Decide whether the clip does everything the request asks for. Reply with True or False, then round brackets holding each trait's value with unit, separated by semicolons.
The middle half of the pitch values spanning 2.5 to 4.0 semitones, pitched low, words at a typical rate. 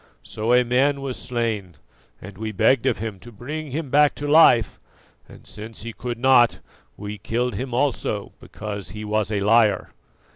True (3.4 semitones; 115 Hz; 175 wpm)